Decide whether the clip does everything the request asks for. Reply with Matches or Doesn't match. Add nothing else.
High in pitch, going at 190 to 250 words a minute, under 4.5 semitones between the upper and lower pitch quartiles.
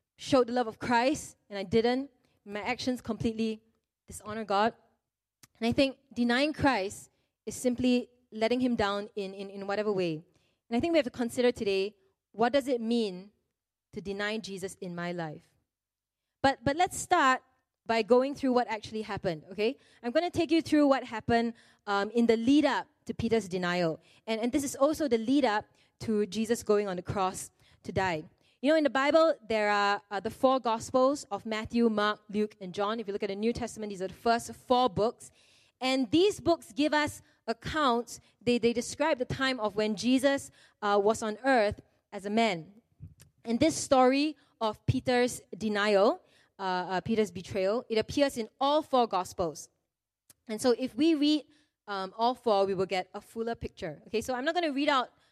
Matches